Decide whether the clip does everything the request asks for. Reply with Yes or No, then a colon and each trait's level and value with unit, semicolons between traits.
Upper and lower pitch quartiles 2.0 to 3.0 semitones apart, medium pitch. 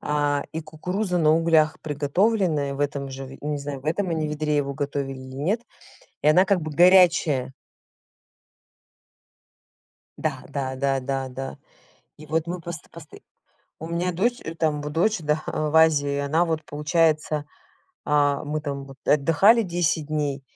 Yes: average, 2.7 semitones; medium, 150 Hz